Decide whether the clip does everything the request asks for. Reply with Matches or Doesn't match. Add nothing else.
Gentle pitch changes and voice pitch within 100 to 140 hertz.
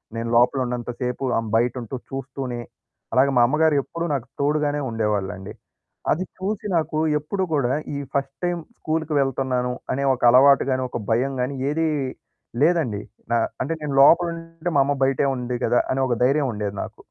Doesn't match